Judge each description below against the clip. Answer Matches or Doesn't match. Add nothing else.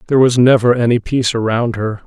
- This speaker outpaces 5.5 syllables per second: Matches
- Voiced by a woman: Doesn't match